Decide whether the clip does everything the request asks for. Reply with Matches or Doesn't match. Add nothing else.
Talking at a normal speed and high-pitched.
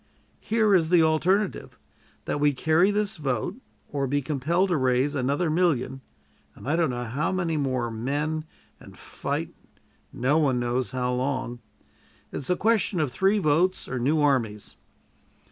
Doesn't match